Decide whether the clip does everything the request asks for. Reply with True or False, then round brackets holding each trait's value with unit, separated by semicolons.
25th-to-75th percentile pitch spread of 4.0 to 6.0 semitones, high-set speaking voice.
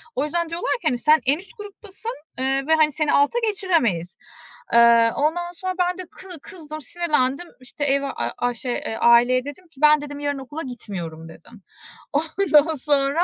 True (5.1 semitones; 290 Hz)